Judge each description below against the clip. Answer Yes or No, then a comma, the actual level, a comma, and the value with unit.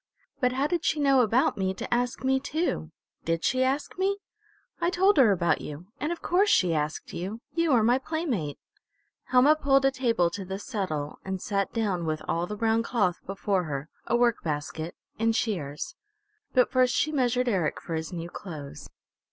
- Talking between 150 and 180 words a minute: No, average, 190 wpm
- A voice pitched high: Yes, high, 225 Hz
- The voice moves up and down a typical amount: No, wide, 7.4 semitones